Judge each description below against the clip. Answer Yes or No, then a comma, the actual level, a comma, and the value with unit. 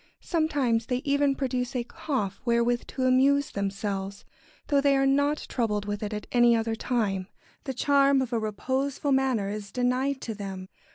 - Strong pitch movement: No, average, 4.4 semitones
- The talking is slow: No, average, 170 wpm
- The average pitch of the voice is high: Yes, very high, 250 Hz